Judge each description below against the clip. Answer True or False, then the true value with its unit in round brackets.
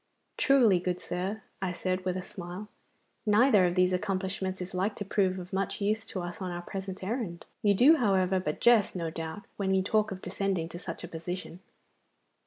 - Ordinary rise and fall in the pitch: False (2.2 semitones)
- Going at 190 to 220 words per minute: True (195 wpm)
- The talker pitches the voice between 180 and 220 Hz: True (190 Hz)